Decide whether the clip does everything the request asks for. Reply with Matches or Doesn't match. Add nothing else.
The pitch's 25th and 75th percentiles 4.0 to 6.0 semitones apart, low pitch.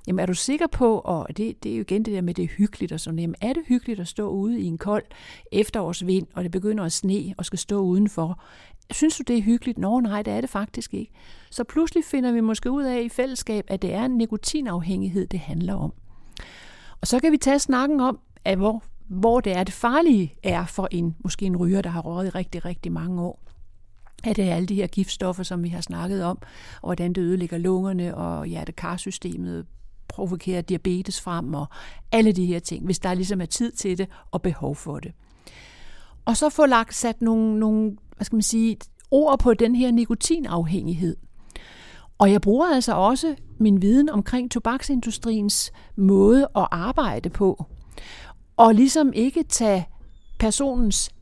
Doesn't match